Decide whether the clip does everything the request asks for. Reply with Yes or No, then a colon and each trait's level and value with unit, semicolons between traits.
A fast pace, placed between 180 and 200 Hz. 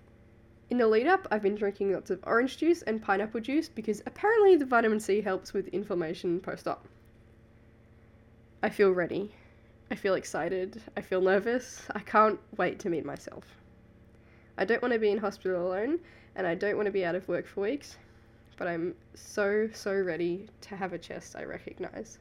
No: average, 185 wpm; high, 190 Hz